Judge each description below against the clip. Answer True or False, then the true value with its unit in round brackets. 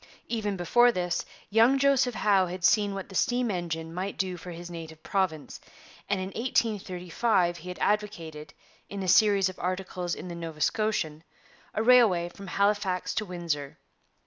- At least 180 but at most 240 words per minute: False (165 wpm)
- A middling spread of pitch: True (3.3 semitones)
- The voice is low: False (185 Hz)